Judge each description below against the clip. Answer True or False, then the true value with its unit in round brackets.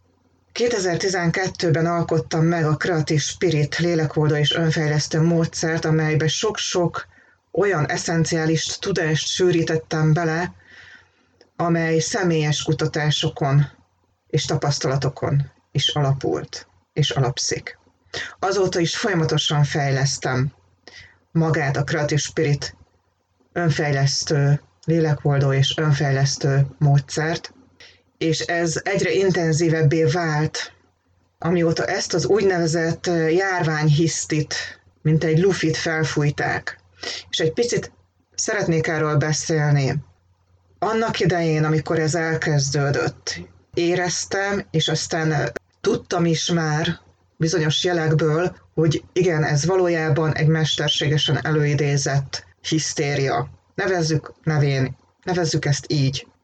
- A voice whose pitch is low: False (155 Hz)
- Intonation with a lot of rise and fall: False (2.7 semitones)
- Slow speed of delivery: True (90 wpm)